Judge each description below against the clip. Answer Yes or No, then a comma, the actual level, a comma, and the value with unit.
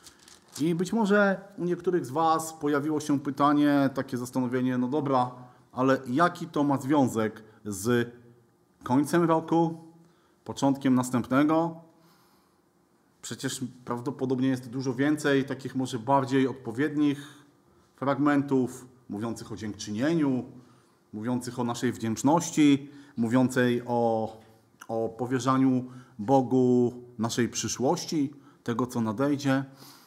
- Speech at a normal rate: No, slow, 100 wpm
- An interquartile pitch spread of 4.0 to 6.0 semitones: No, average, 3.1 semitones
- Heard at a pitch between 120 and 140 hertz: Yes, low, 130 Hz